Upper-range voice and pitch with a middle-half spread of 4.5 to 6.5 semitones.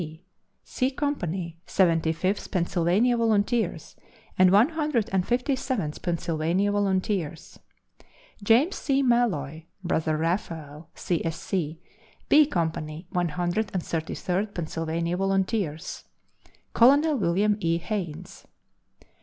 No: medium, 180 Hz; average, 5.1 semitones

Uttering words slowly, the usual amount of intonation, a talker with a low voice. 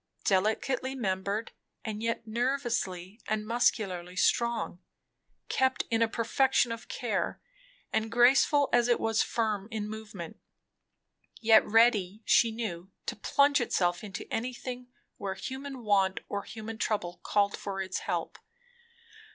No: slow, 125 wpm; average, 3.3 semitones; high, 220 Hz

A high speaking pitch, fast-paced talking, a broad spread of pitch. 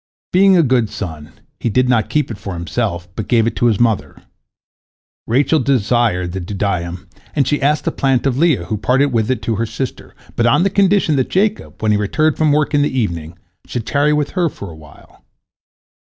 No: low, 120 Hz; fast, 210 wpm; wide, 6.2 semitones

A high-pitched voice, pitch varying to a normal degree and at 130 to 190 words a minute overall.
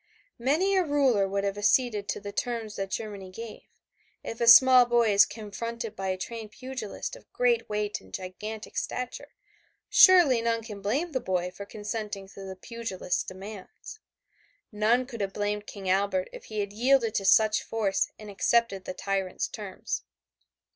Yes: high, 215 Hz; average, 3.1 semitones; average, 170 wpm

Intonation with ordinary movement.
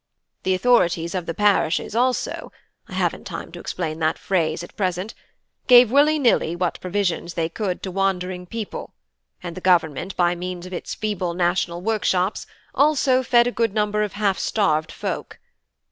Yes: average, 3.7 semitones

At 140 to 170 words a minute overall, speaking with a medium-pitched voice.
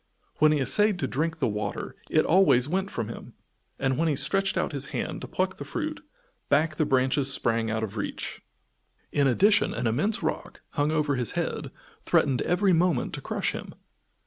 No: average, 190 wpm; medium, 150 Hz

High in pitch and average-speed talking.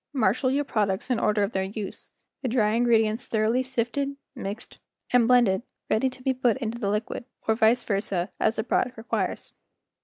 Yes: high, 225 Hz; average, 190 wpm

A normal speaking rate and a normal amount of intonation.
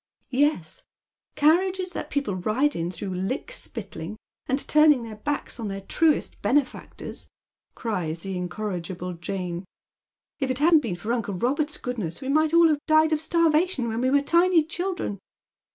No: average, 170 wpm; wide, 8.0 semitones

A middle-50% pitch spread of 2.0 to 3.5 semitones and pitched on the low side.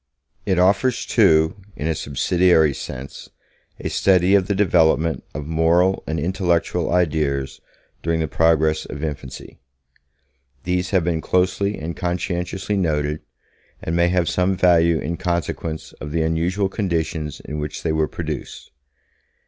Yes: narrow, 2.5 semitones; very low, 85 Hz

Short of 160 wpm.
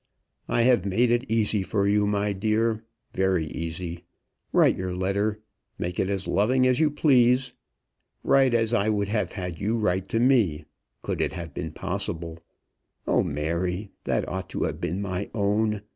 No: average, 170 wpm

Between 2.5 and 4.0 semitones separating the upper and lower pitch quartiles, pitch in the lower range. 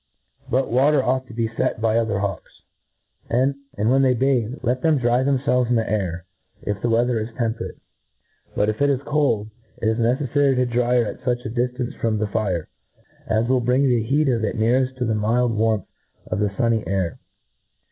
Yes: average, 2.8 semitones; low, 120 Hz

